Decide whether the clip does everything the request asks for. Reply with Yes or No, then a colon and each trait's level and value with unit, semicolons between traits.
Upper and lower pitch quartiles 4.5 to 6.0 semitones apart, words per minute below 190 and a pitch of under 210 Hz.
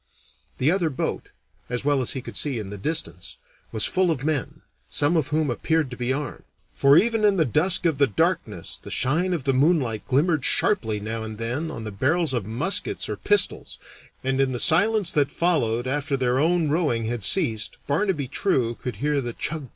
No: average, 5.2 semitones; average, 200 wpm; medium, 140 Hz